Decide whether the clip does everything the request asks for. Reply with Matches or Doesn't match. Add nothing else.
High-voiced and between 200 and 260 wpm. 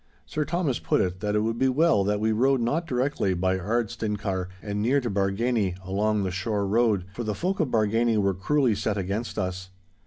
Doesn't match